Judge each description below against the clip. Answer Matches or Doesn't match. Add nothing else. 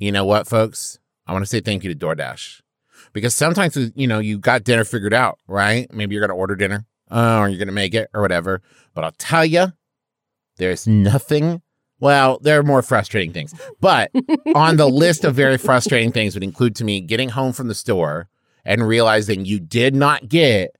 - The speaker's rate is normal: Doesn't match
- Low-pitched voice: Matches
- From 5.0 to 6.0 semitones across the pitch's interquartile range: Matches